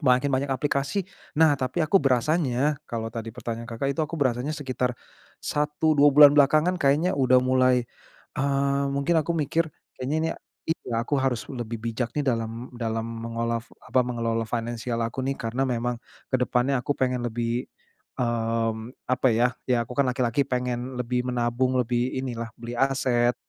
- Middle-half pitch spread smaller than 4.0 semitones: Yes, average, 2.9 semitones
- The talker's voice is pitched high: No, low, 125 Hz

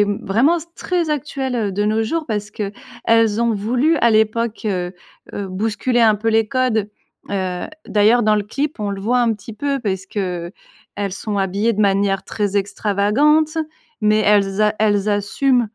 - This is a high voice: Yes, high, 215 Hz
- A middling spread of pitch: Yes, average, 3.0 semitones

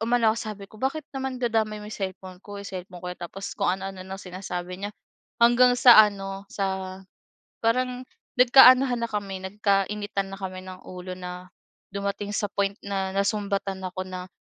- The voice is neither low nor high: No, high, 200 Hz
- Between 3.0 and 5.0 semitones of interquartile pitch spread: No, narrow, 2.5 semitones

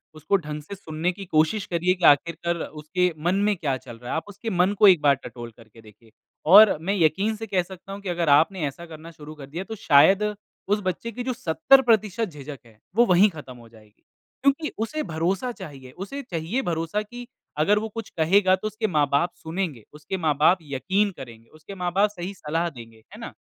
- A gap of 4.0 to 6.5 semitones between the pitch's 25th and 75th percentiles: Yes, average, 5.1 semitones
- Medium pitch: Yes, medium, 175 Hz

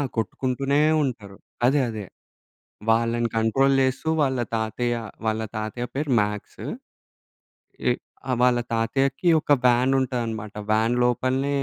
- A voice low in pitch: Yes, low, 120 Hz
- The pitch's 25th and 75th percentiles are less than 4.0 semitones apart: Yes, average, 3.1 semitones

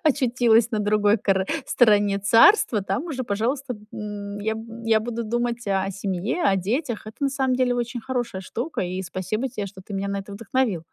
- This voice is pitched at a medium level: No, high, 220 Hz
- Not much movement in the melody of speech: No, average, 3.5 semitones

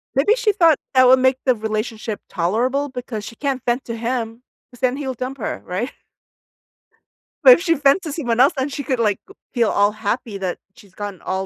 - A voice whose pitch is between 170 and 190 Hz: No, very high, 250 Hz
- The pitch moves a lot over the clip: No, average, 4.1 semitones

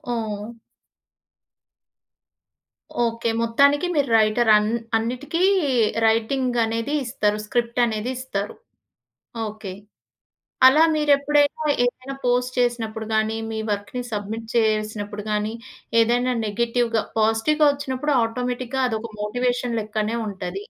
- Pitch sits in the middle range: No, high, 230 Hz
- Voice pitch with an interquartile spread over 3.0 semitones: No, average, 2.7 semitones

